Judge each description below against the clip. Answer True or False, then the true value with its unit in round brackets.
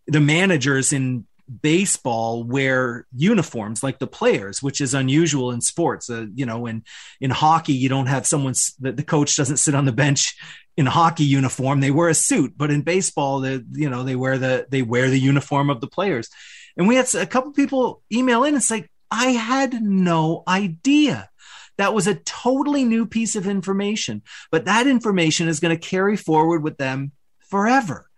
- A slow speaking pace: False (190 wpm)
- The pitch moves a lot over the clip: True (6.5 semitones)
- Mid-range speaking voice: True (150 Hz)